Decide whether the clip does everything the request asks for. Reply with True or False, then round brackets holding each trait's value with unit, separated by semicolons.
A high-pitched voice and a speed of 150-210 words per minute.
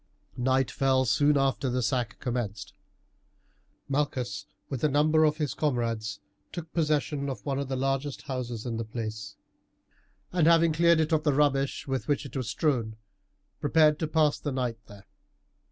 False (135 Hz; 165 wpm)